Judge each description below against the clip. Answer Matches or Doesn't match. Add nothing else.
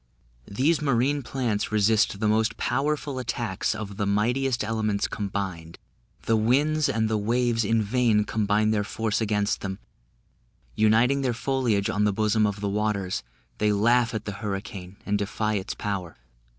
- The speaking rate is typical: Matches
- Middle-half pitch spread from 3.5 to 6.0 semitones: Doesn't match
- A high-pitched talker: Doesn't match